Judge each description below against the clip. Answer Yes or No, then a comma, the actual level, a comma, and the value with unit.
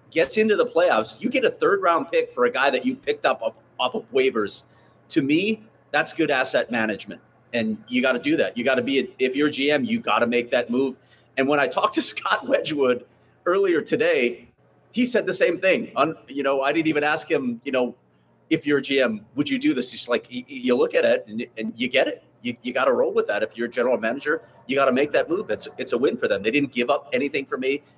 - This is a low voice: No, high, 210 Hz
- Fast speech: Yes, fast, 255 wpm